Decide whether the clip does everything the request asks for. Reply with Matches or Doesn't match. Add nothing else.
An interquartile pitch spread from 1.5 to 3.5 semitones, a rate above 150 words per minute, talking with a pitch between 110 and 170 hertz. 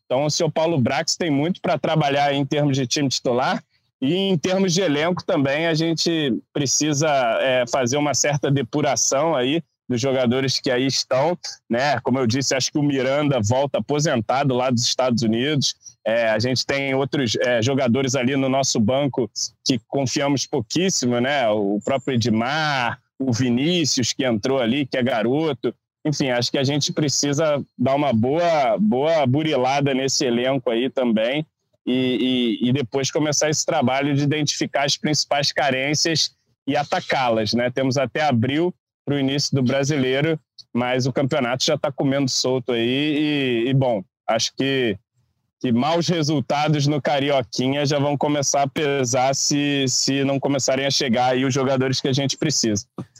Matches